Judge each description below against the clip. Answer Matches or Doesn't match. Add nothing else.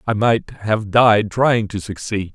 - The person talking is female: Doesn't match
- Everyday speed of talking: Matches